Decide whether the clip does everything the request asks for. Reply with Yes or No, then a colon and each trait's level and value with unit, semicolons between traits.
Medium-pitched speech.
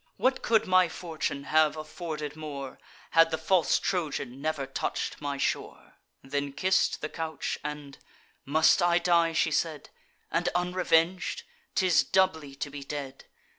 Yes: medium, 155 Hz